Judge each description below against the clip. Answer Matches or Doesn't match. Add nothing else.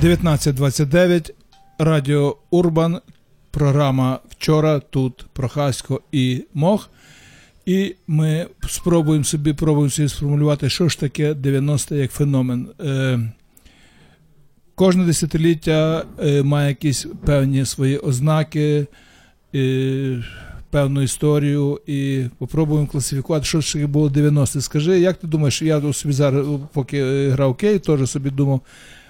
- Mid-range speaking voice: Matches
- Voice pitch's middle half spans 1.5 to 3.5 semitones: Matches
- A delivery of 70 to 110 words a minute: Matches